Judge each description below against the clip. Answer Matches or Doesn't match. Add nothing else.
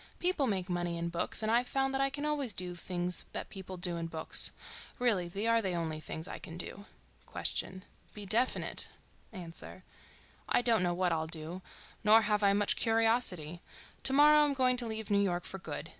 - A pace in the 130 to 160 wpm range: Doesn't match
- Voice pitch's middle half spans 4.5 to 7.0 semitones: Matches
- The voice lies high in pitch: Matches